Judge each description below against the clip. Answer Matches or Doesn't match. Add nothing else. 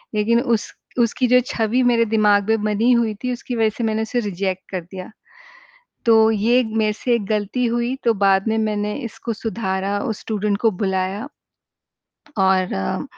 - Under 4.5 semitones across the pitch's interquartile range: Matches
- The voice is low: Doesn't match